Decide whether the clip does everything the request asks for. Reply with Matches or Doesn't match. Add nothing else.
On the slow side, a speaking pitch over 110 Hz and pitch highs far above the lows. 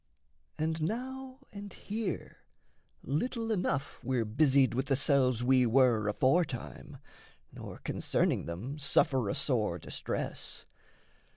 Matches